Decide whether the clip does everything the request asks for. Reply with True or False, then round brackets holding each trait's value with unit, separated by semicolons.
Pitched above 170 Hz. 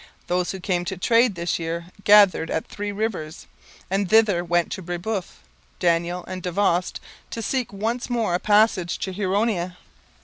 True (185 Hz)